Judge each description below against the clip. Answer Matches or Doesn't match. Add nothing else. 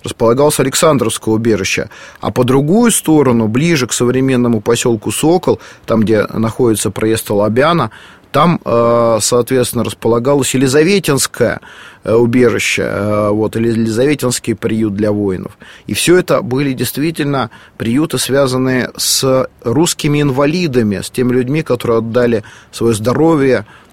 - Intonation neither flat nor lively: Matches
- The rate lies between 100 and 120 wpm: Matches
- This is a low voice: Matches